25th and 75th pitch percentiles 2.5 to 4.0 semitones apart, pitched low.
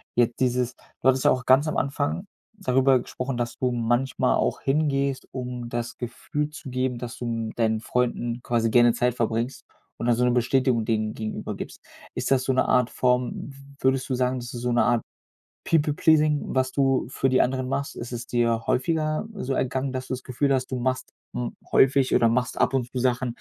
No: narrow, 1.9 semitones; low, 125 Hz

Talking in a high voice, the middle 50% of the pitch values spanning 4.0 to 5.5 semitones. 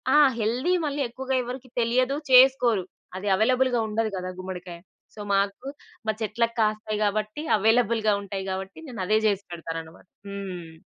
Yes: high, 215 Hz; average, 4.3 semitones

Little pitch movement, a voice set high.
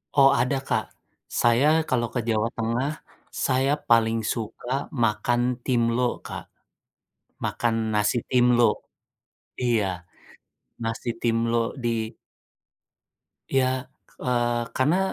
No: narrow, 2.0 semitones; low, 120 Hz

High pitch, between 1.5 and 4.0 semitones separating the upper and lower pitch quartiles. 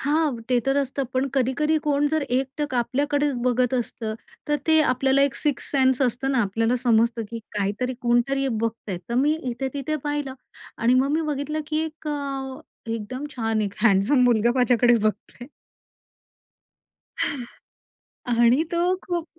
Yes: very high, 260 Hz; average, 3.4 semitones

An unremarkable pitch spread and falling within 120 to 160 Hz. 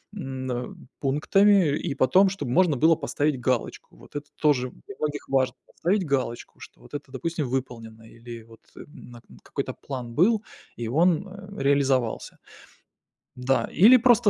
No: wide, 5.8 semitones; medium, 140 Hz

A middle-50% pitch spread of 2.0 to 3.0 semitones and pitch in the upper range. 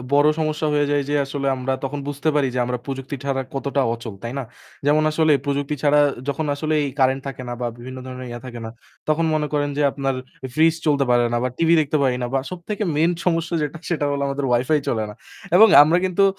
No: average, 2.7 semitones; medium, 145 Hz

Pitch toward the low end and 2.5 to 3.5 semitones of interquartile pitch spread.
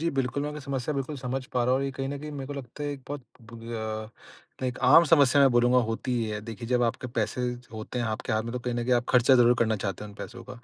Yes: low, 125 Hz; average, 2.9 semitones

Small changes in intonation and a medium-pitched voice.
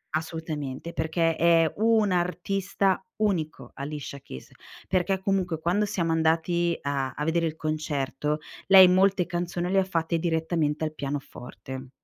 No: average, 3.0 semitones; medium, 165 Hz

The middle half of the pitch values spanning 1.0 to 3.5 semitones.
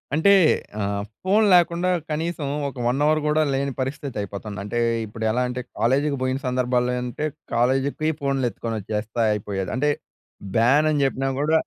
No: average, 4.6 semitones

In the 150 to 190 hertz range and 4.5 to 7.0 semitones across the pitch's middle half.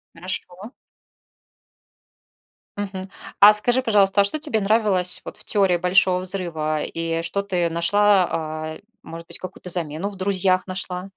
No: medium, 185 Hz; average, 2.9 semitones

